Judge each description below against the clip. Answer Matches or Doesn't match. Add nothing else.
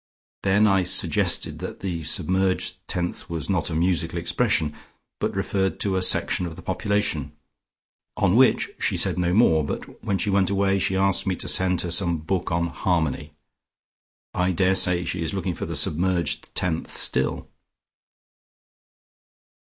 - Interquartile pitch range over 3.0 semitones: Doesn't match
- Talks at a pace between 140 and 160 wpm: Matches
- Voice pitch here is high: Doesn't match